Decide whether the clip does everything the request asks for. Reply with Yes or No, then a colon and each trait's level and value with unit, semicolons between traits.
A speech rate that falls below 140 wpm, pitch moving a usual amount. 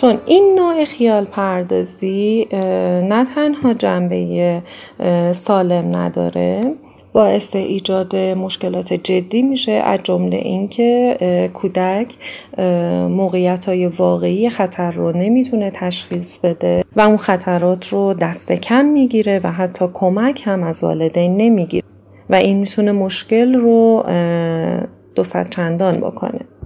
Yes: average, 110 wpm; average, 4.1 semitones